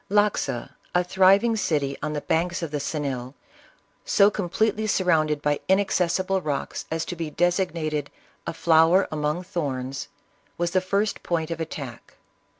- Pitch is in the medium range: Yes, medium, 165 Hz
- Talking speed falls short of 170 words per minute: Yes, average, 150 wpm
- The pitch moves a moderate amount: Yes, average, 3.9 semitones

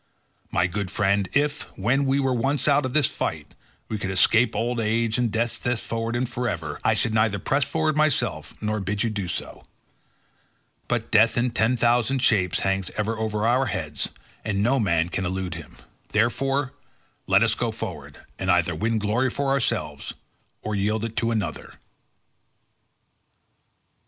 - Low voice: Yes, low, 110 Hz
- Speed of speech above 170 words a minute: No, average, 165 wpm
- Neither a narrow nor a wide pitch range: Yes, average, 4.1 semitones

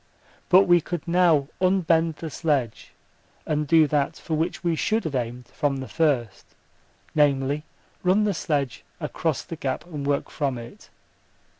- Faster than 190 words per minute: No, average, 155 wpm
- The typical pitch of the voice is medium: Yes, medium, 150 Hz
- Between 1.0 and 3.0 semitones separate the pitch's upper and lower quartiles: No, average, 3.5 semitones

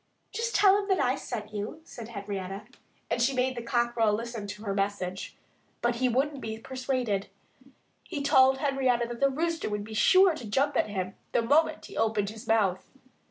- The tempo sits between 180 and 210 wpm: Yes, average, 190 wpm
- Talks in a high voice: Yes, high, 235 Hz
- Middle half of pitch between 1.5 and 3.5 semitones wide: No, average, 4.5 semitones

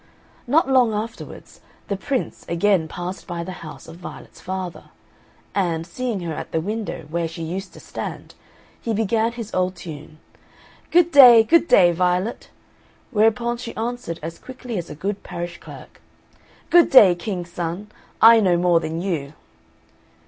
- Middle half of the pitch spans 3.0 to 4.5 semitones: No, average, 5.1 semitones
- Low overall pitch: No, high, 190 Hz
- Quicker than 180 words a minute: No, average, 155 wpm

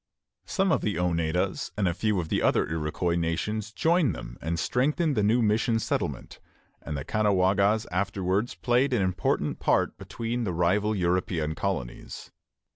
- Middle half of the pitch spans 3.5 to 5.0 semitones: Yes, average, 4.5 semitones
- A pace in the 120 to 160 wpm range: Yes, average, 155 wpm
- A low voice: Yes, low, 100 Hz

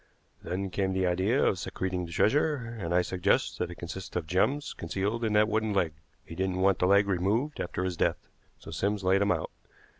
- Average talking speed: No, fast, 210 wpm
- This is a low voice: Yes, very low, 95 Hz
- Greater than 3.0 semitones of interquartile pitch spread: No, average, 2.7 semitones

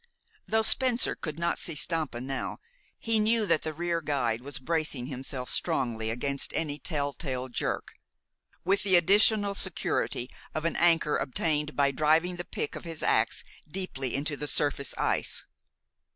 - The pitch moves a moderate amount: Yes, average, 4.2 semitones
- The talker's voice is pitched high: No, medium, 155 Hz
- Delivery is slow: No, average, 155 wpm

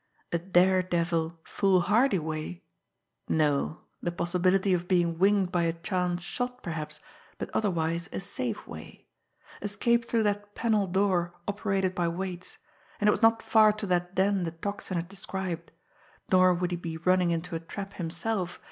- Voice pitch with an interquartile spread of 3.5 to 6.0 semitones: No, average, 2.8 semitones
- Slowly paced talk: No, average, 155 wpm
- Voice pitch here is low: No, medium, 180 Hz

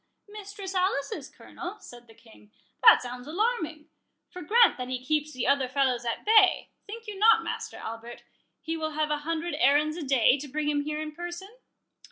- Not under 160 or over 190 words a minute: Yes, average, 180 wpm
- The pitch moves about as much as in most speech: No, wide, 6.3 semitones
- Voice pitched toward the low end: No, very high, 305 Hz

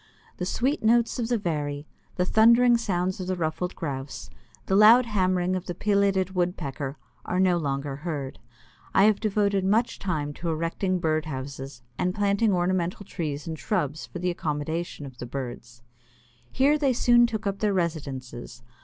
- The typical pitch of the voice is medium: Yes, medium, 180 Hz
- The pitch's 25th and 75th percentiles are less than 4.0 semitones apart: No, wide, 5.5 semitones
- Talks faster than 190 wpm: No, average, 165 wpm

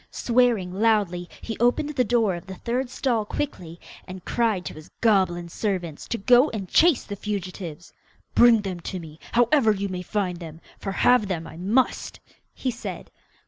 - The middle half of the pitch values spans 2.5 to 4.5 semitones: No, average, 4.9 semitones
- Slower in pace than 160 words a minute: No, average, 175 wpm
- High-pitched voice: Yes, high, 200 Hz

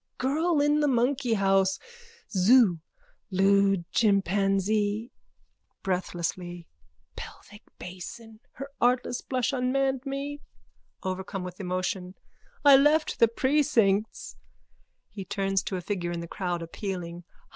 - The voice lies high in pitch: Yes, high, 200 Hz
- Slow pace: Yes, slow, 105 wpm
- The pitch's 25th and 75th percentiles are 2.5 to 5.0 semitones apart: No, wide, 5.5 semitones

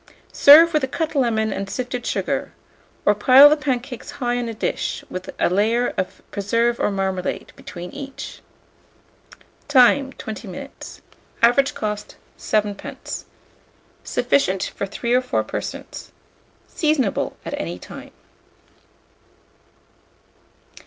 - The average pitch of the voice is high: Yes, high, 240 Hz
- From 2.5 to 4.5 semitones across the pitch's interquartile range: No, average, 5.1 semitones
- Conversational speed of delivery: No, slow, 120 wpm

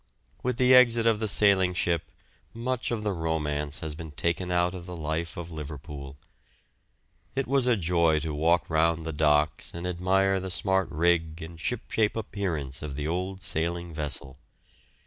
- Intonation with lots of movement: No, average, 3.7 semitones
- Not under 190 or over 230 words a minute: No, average, 165 wpm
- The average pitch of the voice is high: No, very low, 85 Hz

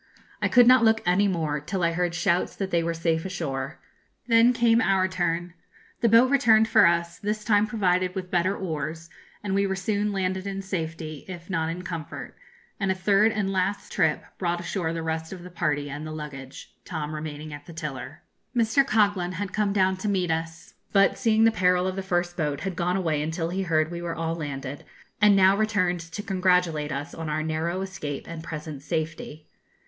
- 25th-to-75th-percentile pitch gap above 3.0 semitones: Yes, average, 3.4 semitones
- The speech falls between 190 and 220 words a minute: Yes, fast, 205 wpm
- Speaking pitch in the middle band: Yes, medium, 175 Hz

